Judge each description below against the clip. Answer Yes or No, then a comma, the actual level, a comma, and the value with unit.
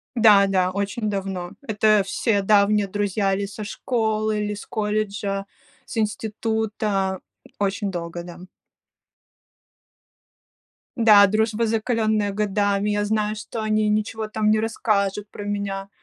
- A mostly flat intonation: Yes, narrow, 1.5 semitones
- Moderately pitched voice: No, high, 210 Hz